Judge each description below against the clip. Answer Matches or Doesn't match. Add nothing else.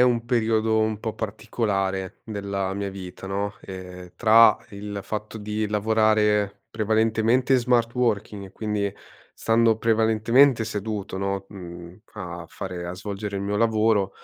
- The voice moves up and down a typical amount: Doesn't match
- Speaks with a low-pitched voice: Matches